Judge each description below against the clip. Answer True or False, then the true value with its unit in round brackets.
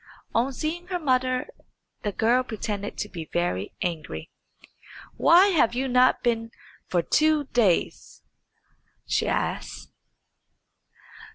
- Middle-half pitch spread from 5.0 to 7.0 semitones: True (5.6 semitones)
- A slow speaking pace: True (110 wpm)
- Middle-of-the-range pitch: False (245 Hz)